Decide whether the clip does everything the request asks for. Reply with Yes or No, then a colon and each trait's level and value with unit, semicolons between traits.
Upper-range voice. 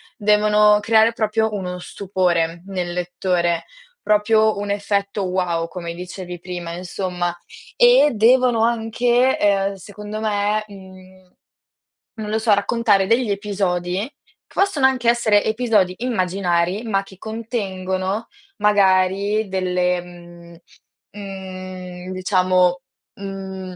Yes: high, 195 Hz